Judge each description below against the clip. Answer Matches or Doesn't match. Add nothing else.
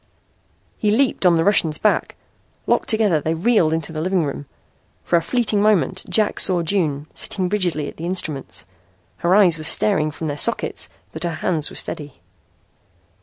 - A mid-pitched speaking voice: Matches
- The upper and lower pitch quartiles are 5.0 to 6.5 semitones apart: Doesn't match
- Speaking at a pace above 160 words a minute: Matches